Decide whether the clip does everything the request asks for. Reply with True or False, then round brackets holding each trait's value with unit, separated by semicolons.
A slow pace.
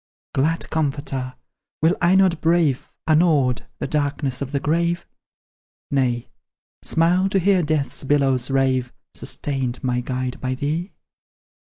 True (125 wpm)